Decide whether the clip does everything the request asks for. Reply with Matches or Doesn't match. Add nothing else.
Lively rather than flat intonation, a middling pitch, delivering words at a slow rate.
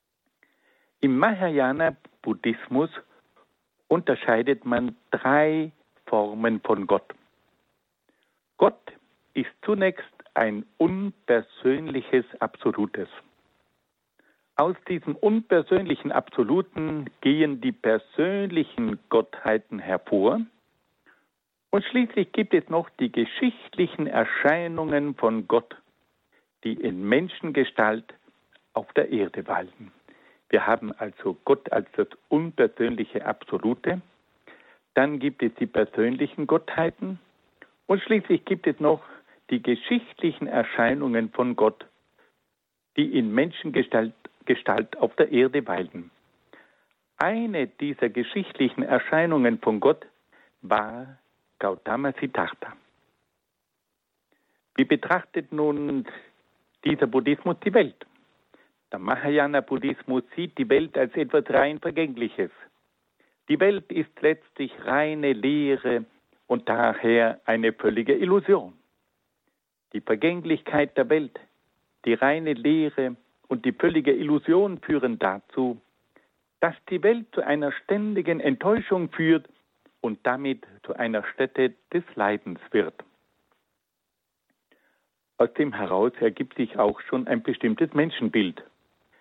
Matches